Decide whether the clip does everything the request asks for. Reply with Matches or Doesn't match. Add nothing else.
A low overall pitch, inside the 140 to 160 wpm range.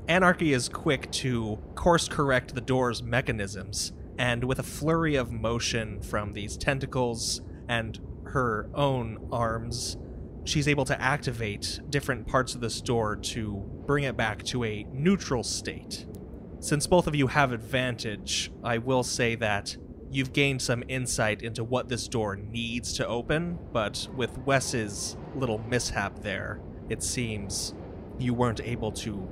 Matches